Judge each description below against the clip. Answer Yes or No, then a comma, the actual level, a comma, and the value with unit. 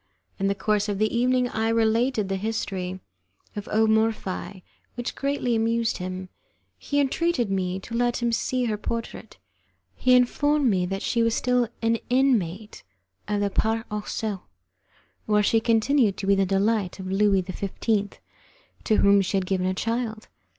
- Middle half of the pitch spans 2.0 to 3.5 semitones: Yes, average, 3.2 semitones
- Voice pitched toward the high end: Yes, high, 220 Hz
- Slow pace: No, average, 165 wpm